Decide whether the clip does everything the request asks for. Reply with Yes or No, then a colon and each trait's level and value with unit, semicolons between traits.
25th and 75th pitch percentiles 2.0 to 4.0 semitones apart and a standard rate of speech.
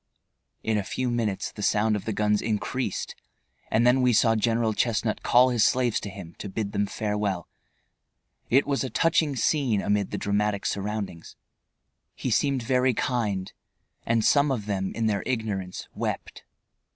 Yes: average, 3.3 semitones; average, 165 wpm